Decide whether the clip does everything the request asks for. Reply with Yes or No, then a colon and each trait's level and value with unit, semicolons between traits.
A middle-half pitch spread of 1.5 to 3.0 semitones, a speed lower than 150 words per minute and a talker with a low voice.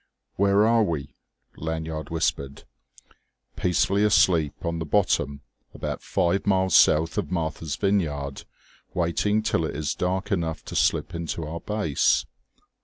No: average, 3.9 semitones; slow, 135 wpm; very low, 85 Hz